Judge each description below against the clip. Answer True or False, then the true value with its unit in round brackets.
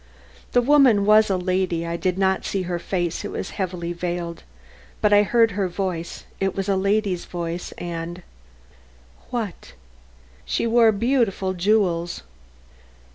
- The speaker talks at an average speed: True (145 wpm)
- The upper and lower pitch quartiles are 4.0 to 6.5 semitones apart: False (3.2 semitones)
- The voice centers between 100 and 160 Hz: False (185 Hz)